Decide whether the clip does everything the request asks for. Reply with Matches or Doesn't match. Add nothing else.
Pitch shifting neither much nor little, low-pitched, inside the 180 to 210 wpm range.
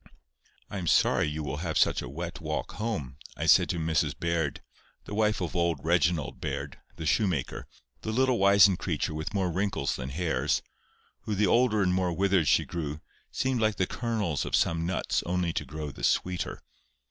Matches